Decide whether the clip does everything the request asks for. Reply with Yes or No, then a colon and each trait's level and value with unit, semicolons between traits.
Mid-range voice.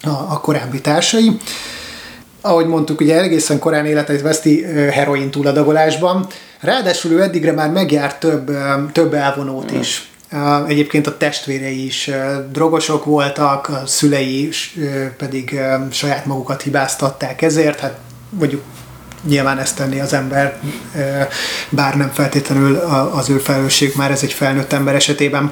Yes: medium, 145 Hz